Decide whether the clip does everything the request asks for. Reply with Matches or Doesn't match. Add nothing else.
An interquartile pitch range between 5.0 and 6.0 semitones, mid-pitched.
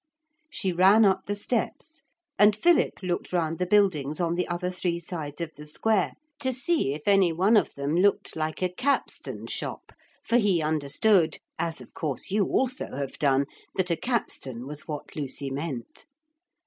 Matches